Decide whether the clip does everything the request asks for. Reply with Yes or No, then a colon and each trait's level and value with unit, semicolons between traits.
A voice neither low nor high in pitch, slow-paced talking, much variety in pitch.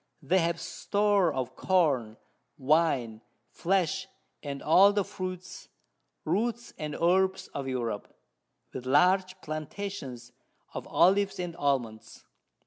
Yes: medium, 165 Hz; slow, 110 wpm; wide, 6.2 semitones